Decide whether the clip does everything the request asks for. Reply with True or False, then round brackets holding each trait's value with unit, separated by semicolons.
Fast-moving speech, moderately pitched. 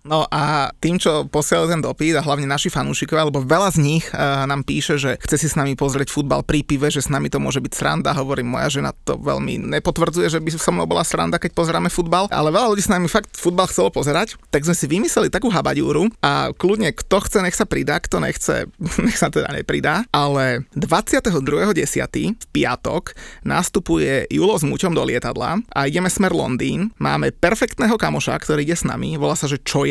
True (205 wpm; 155 Hz)